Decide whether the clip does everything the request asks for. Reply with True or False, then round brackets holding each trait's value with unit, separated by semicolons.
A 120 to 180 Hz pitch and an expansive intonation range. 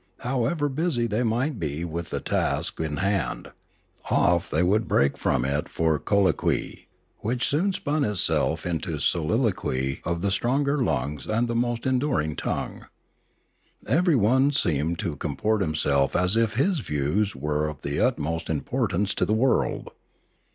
False (100 Hz; 8.0 semitones)